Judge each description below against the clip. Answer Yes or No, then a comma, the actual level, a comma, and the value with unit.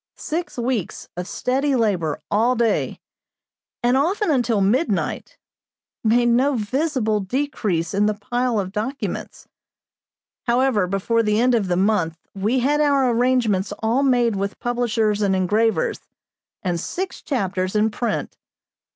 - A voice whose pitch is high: Yes, high, 230 Hz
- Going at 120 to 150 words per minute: Yes, slow, 135 wpm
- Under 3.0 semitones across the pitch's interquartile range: No, average, 4.0 semitones